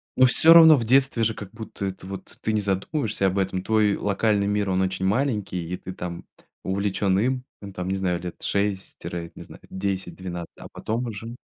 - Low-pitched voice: Yes, low, 100 Hz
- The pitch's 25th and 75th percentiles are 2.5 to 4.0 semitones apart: Yes, average, 2.9 semitones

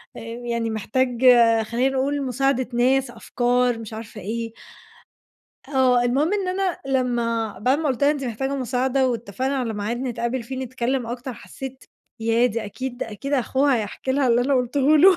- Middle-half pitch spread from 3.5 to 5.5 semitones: No, narrow, 2.5 semitones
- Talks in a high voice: Yes, very high, 250 Hz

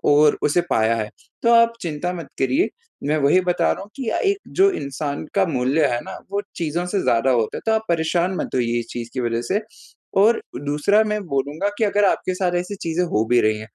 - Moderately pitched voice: Yes, medium, 165 Hz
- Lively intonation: Yes, wide, 7.2 semitones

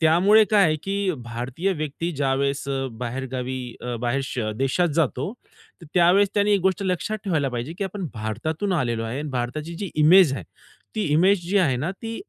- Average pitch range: No, wide, 6.5 semitones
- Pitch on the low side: No, medium, 155 Hz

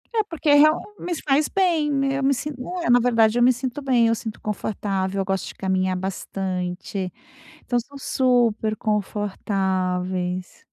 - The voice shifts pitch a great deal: Yes, wide, 6.2 semitones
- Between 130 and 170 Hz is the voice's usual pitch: No, high, 225 Hz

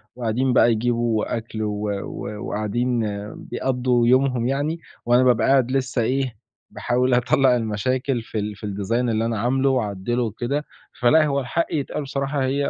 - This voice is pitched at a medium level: No, low, 125 Hz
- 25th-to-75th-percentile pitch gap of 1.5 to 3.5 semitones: Yes, average, 2.8 semitones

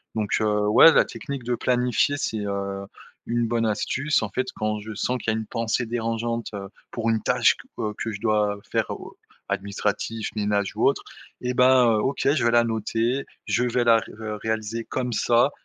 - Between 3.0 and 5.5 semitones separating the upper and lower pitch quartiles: No, narrow, 2.4 semitones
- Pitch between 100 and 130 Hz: Yes, low, 115 Hz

